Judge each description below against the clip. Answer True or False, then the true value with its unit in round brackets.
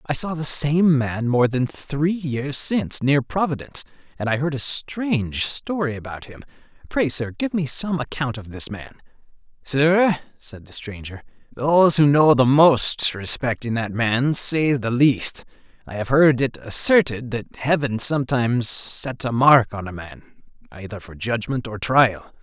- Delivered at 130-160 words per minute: False (170 wpm)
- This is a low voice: True (130 Hz)